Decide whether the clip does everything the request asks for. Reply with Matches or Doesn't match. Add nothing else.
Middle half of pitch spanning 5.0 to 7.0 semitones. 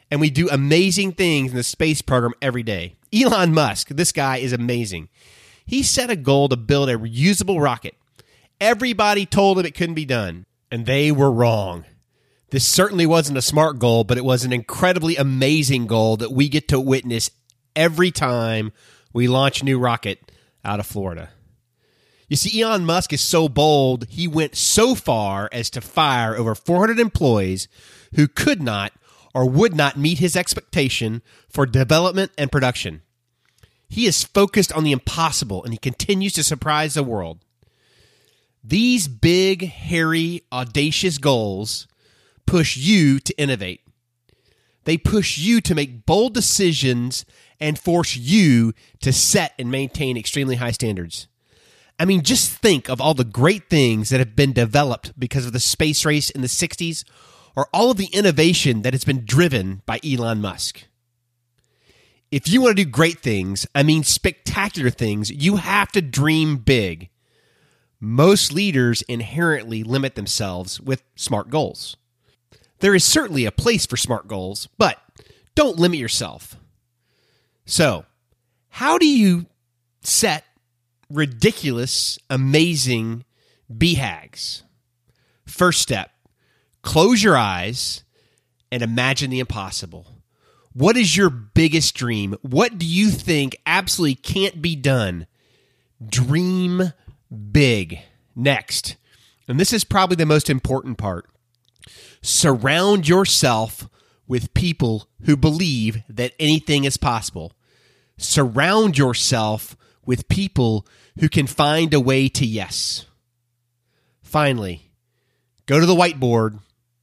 Matches